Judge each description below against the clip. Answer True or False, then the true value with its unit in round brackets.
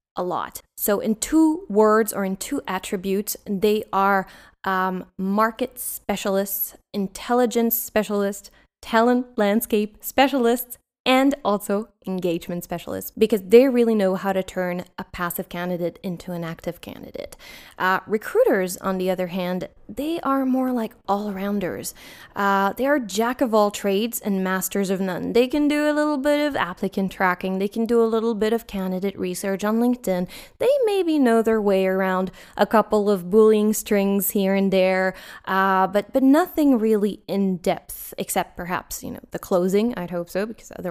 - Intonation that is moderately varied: True (3.6 semitones)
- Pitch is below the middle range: False (205 Hz)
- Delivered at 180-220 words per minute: False (165 wpm)